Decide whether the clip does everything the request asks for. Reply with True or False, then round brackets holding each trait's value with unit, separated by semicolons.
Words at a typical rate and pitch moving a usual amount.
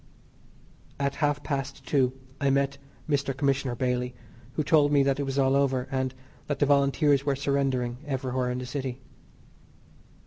False (160 wpm; 1.4 semitones)